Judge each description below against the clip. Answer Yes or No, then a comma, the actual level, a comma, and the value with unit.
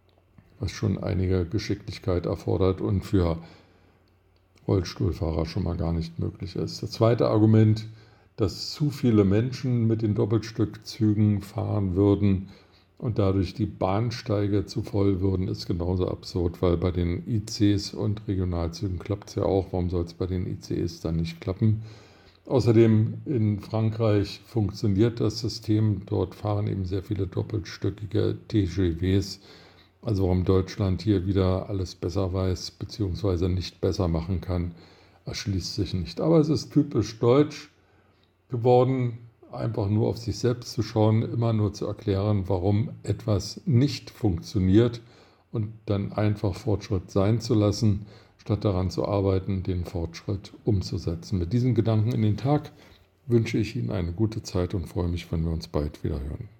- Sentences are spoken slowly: No, average, 150 wpm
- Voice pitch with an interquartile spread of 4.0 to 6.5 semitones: No, average, 2.9 semitones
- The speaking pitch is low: Yes, low, 100 Hz